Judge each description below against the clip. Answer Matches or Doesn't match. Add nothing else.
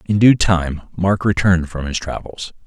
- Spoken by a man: Matches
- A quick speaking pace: Doesn't match